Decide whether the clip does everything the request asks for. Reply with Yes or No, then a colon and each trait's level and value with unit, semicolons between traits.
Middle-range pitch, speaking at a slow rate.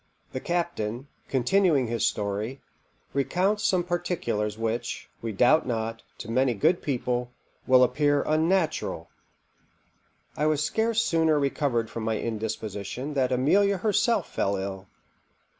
No: low, 130 Hz; slow, 125 wpm